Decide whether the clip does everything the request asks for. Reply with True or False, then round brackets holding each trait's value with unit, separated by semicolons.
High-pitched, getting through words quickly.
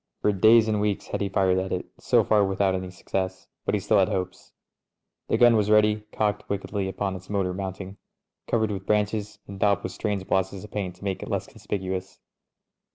False (100 Hz; 210 wpm)